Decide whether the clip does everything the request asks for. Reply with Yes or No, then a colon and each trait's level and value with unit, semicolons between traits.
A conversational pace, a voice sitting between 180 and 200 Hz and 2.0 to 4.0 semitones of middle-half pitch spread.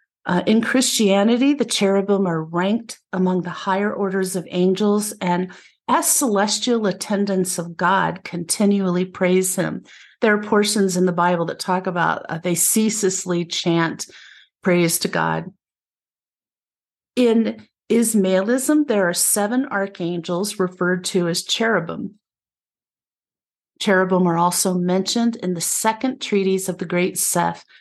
No: slow, 130 wpm; high, 190 Hz; average, 3.0 semitones